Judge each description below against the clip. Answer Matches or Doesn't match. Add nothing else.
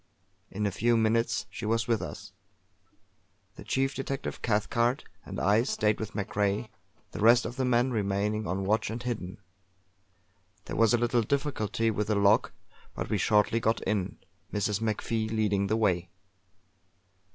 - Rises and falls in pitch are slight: Matches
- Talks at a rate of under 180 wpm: Matches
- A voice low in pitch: Matches